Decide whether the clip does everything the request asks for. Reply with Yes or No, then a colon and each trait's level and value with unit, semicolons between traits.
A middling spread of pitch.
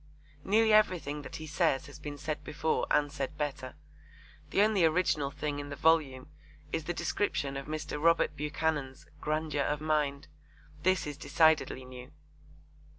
No: narrow, 2.0 semitones